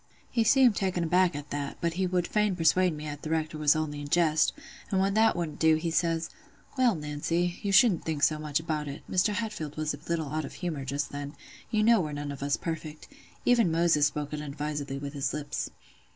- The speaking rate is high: Yes, fast, 215 wpm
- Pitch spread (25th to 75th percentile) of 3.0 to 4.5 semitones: Yes, average, 3.6 semitones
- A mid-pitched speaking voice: Yes, medium, 160 Hz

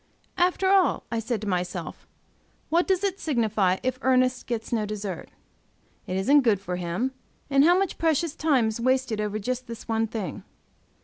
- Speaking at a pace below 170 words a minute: No, average, 175 wpm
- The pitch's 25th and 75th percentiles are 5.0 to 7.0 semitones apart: Yes, average, 5.3 semitones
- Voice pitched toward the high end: Yes, high, 235 Hz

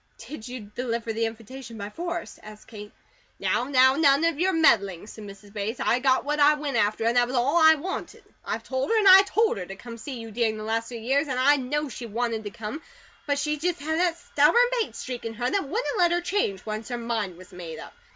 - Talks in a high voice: Yes, very high, 250 Hz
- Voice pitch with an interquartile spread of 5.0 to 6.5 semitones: Yes, wide, 5.4 semitones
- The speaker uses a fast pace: Yes, fast, 240 wpm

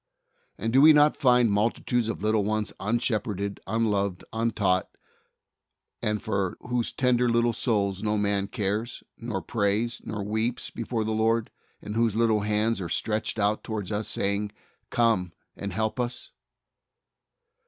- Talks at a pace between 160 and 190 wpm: No, average, 145 wpm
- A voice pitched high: No, low, 110 Hz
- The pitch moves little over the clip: Yes, narrow, 2.3 semitones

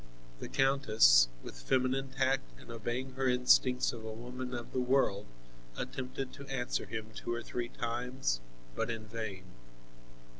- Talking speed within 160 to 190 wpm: No, average, 150 wpm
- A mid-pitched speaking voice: No, low, 125 Hz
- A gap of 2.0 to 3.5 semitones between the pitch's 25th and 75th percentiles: Yes, average, 2.8 semitones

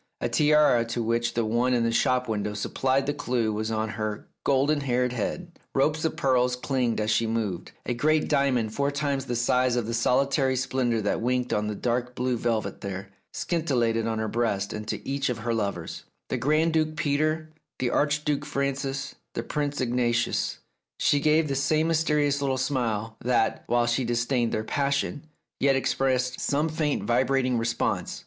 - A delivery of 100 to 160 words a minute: No, average, 180 wpm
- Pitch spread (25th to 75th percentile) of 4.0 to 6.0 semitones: No, average, 3.4 semitones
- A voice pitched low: Yes, low, 125 Hz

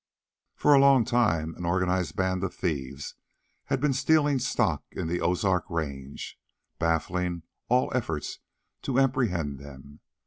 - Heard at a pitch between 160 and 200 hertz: No, very low, 90 Hz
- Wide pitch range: Yes, wide, 7.8 semitones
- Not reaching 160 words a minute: Yes, slow, 135 wpm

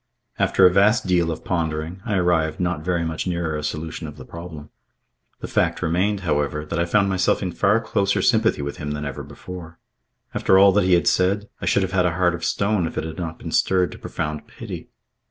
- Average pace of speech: No, fast, 225 wpm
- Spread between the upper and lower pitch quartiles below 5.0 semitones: Yes, average, 3.1 semitones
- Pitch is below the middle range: Yes, very low, 90 Hz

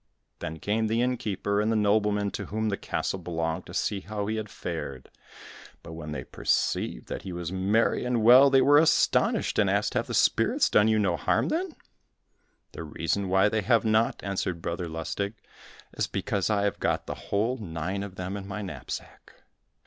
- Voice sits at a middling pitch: No, low, 100 Hz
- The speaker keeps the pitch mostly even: No, average, 3.4 semitones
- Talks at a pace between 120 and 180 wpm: No, average, 195 wpm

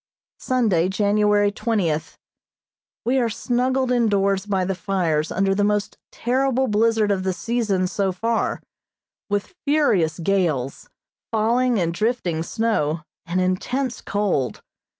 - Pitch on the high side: Yes, high, 205 Hz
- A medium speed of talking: No, slow, 120 wpm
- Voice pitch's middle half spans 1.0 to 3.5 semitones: No, average, 4.1 semitones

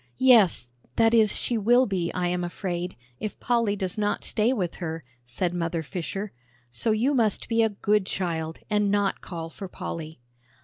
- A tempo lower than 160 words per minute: No, average, 175 wpm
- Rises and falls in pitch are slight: No, average, 4.0 semitones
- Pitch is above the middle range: Yes, high, 195 Hz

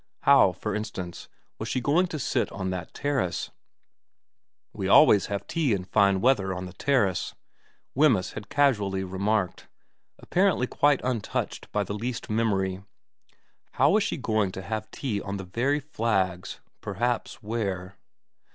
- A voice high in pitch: No, low, 105 Hz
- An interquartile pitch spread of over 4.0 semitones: Yes, average, 5.2 semitones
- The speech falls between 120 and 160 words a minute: Yes, average, 150 wpm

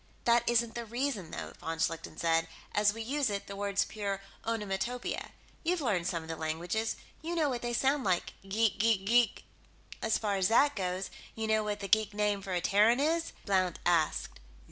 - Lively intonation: No, average, 3.9 semitones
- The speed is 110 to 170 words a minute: No, average, 195 wpm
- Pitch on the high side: Yes, high, 210 Hz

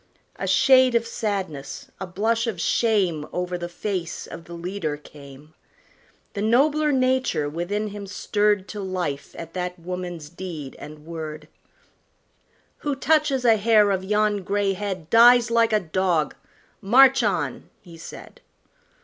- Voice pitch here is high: Yes, high, 195 Hz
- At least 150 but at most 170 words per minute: No, average, 140 wpm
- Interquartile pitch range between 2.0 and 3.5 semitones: No, average, 5.2 semitones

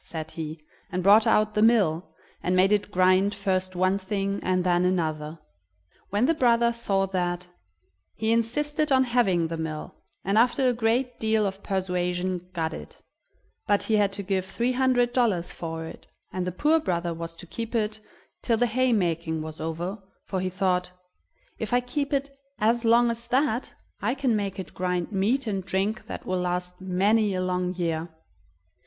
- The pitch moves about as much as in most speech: Yes, average, 4.4 semitones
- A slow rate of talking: No, average, 180 wpm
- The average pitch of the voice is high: Yes, high, 195 Hz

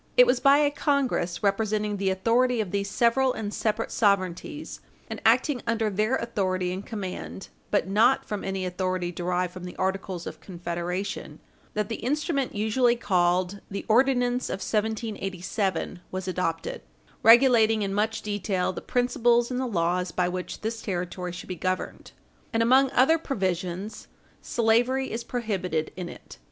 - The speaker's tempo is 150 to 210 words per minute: Yes, average, 155 wpm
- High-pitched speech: Yes, high, 205 Hz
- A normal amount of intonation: Yes, average, 4.4 semitones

